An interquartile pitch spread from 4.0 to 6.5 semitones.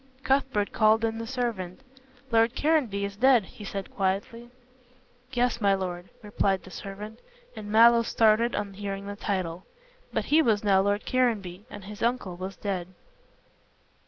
No: average, 3.1 semitones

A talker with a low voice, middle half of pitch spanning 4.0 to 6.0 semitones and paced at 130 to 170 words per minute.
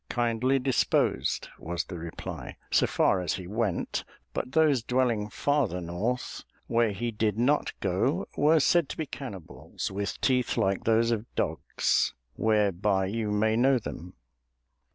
Yes: low, 115 Hz; average, 4.5 semitones; average, 145 wpm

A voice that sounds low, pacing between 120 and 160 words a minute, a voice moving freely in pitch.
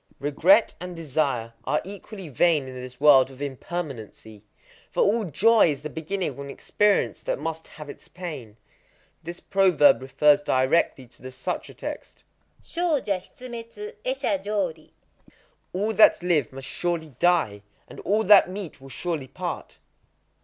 No: medium, 160 Hz; average, 145 wpm; wide, 6.4 semitones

